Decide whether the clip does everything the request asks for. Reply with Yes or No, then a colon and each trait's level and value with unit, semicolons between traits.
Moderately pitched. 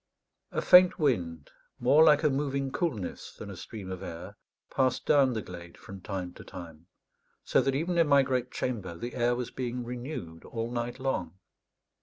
No: low, 120 Hz